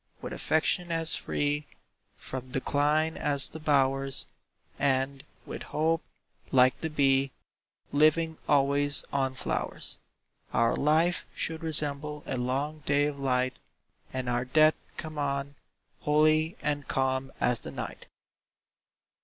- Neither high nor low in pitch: Yes, medium, 145 Hz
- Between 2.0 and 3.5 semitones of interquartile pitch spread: Yes, narrow, 2.5 semitones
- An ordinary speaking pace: No, slow, 120 wpm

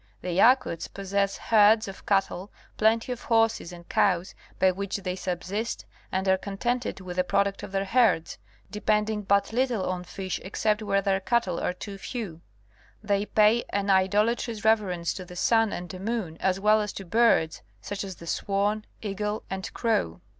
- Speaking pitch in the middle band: No, high, 200 Hz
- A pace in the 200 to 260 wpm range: No, average, 170 wpm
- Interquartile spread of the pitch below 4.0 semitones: Yes, narrow, 2.6 semitones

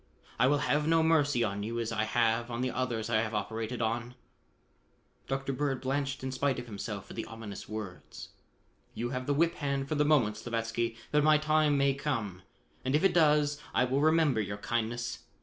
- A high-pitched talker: No, low, 125 Hz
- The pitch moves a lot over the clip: No, average, 4.2 semitones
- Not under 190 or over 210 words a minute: Yes, average, 200 wpm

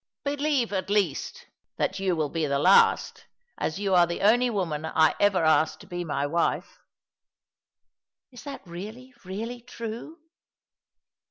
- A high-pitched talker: Yes, high, 195 Hz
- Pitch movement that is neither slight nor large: No, wide, 6.0 semitones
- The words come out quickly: No, average, 155 wpm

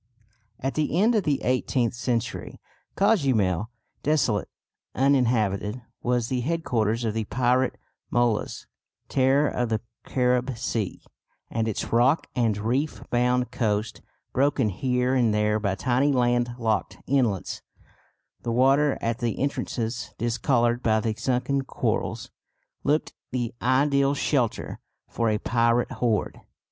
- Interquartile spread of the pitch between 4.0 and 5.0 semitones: No, average, 2.9 semitones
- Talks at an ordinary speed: No, slow, 125 wpm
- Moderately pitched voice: No, low, 120 Hz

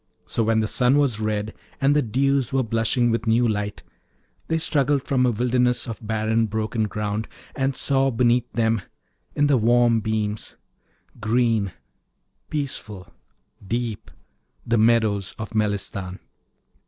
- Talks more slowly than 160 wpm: Yes, slow, 135 wpm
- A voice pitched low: Yes, low, 115 Hz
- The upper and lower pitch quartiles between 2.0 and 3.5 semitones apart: Yes, average, 2.7 semitones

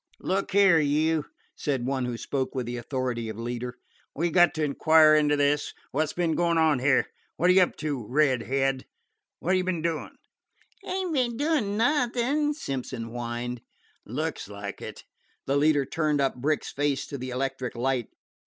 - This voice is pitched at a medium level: Yes, medium, 145 Hz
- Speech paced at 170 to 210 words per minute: Yes, average, 180 wpm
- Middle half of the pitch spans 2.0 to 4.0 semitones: No, average, 4.8 semitones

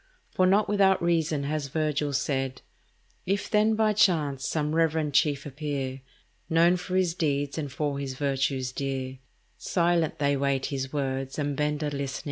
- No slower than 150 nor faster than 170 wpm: Yes, average, 165 wpm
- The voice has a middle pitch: Yes, medium, 145 Hz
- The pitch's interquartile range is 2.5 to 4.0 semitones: Yes, average, 3.3 semitones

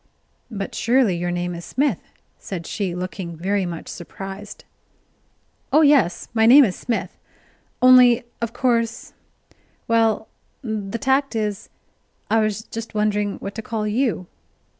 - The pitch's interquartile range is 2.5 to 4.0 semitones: Yes, average, 3.6 semitones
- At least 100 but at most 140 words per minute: Yes, slow, 135 wpm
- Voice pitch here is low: No, high, 215 Hz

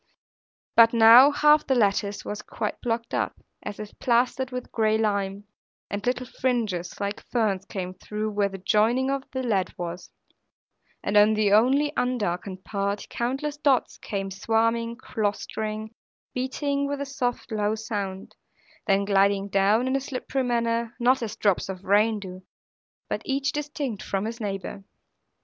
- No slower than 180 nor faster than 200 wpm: No, average, 155 wpm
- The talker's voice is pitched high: Yes, high, 220 Hz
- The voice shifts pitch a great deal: No, average, 3.9 semitones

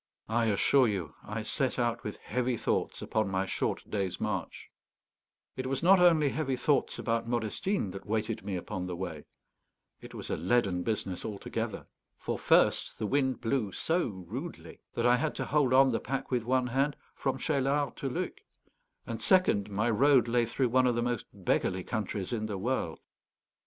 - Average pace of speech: Yes, average, 180 wpm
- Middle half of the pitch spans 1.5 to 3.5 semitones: No, average, 4.4 semitones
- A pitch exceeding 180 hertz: No, low, 120 Hz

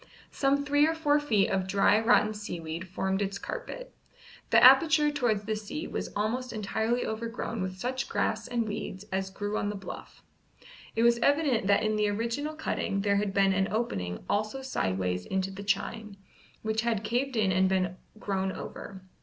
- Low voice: No, high, 215 Hz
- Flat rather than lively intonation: No, average, 3.9 semitones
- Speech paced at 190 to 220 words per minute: No, average, 180 wpm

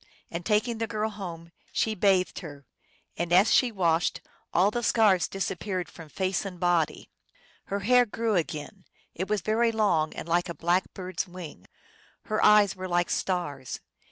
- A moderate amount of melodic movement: Yes, average, 3.6 semitones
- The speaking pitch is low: No, medium, 185 Hz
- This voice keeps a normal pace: Yes, average, 175 wpm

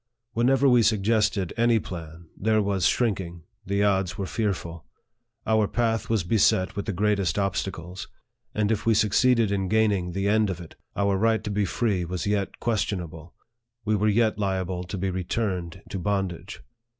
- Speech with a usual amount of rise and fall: Yes, average, 3.1 semitones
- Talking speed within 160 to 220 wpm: Yes, average, 170 wpm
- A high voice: No, low, 100 Hz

